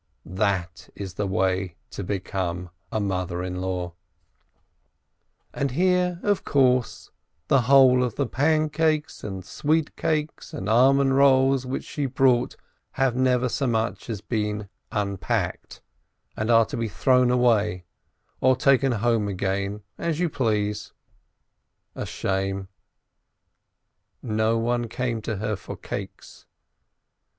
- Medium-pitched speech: No, low, 115 Hz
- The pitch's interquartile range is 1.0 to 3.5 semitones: No, average, 5.3 semitones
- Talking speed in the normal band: No, slow, 125 wpm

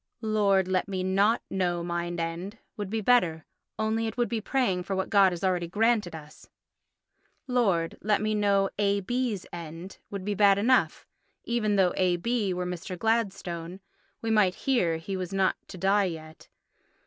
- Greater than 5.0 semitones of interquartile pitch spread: No, average, 3.4 semitones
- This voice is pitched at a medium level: No, high, 195 Hz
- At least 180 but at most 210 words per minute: No, average, 160 wpm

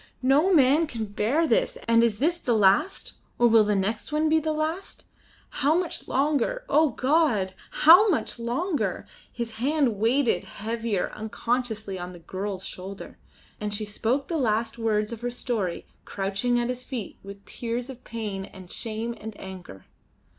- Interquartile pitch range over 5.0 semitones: Yes, wide, 5.5 semitones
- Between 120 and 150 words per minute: No, average, 165 wpm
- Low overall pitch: No, high, 235 Hz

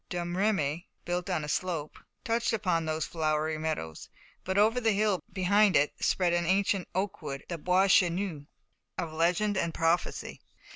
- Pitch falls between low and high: Yes, medium, 175 Hz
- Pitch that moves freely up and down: No, average, 3.7 semitones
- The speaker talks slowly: No, average, 150 wpm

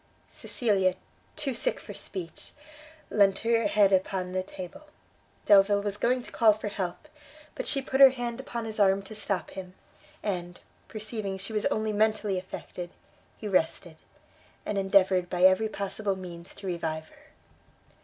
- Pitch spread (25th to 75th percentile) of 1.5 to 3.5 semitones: Yes, average, 2.8 semitones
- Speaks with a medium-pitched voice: No, high, 200 Hz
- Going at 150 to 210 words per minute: Yes, average, 155 wpm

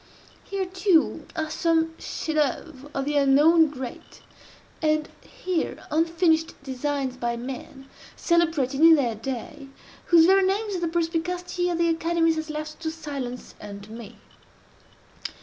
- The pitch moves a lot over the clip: No, average, 3.8 semitones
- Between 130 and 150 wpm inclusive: Yes, slow, 135 wpm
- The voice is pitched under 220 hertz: No, very high, 315 Hz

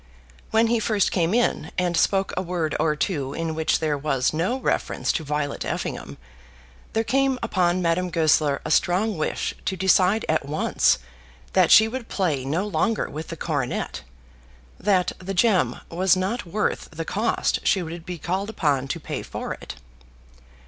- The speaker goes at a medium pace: Yes, average, 170 wpm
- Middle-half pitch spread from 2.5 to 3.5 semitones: No, average, 4.5 semitones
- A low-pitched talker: No, medium, 180 Hz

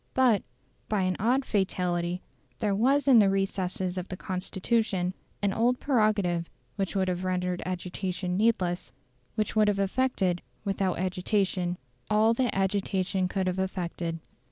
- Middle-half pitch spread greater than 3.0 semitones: No, average, 2.7 semitones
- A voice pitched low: No, high, 190 Hz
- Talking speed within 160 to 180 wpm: No, average, 140 wpm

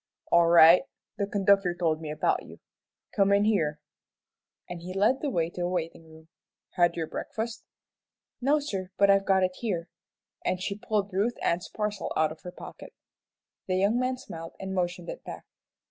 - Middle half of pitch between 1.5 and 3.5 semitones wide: Yes, average, 3.1 semitones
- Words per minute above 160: Yes, average, 180 wpm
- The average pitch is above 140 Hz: Yes, medium, 185 Hz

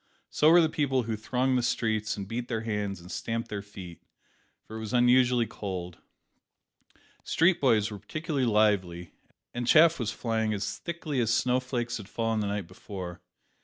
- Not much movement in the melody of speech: No, average, 3.6 semitones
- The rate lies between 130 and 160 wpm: No, average, 175 wpm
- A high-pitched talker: No, low, 115 Hz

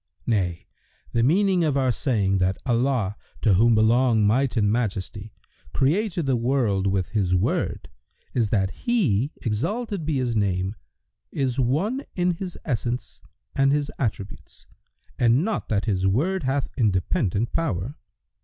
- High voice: No, low, 120 Hz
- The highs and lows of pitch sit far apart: Yes, wide, 5.7 semitones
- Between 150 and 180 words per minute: No, average, 140 wpm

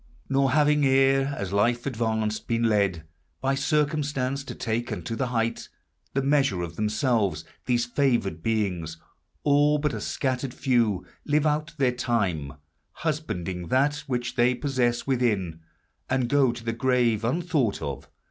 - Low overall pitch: Yes, low, 125 Hz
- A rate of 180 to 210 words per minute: No, average, 145 wpm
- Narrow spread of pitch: No, average, 4.1 semitones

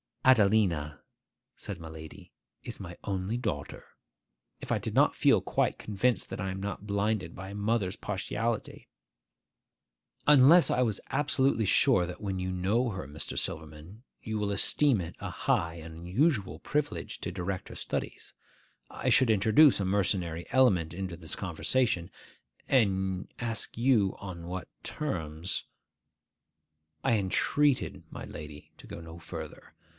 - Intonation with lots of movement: No, average, 4.7 semitones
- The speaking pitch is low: Yes, low, 100 Hz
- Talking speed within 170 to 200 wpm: No, average, 140 wpm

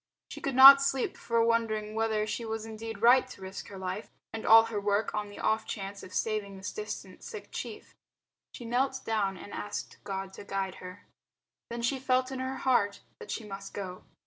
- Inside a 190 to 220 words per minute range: Yes, average, 200 wpm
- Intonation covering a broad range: No, average, 3.5 semitones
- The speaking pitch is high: Yes, high, 220 Hz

